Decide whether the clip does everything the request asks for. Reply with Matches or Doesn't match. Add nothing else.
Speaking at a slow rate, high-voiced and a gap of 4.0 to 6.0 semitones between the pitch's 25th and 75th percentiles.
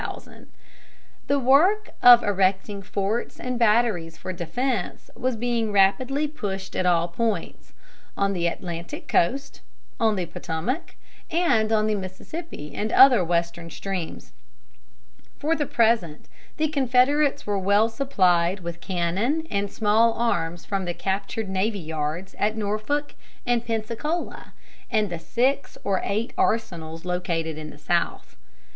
Matches